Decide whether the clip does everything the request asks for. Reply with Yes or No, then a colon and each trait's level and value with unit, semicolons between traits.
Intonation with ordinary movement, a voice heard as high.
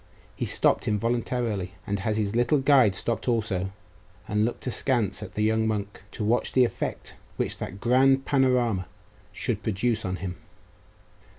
No: average, 3.4 semitones; low, 110 Hz